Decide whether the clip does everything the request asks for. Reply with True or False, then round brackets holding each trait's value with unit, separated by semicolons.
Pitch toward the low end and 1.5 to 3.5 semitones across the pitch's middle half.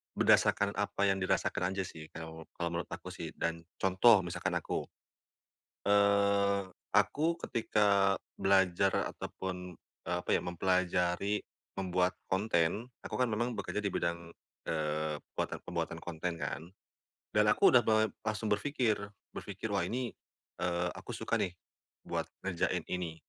True (95 Hz; 2.8 semitones)